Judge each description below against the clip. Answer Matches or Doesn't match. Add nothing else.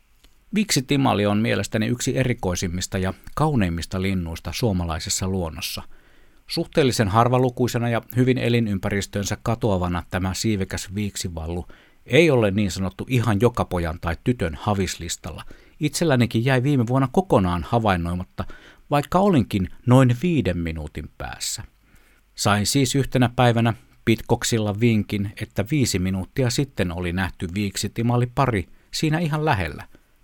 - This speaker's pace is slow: Doesn't match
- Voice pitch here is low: Matches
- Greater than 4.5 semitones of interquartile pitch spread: Matches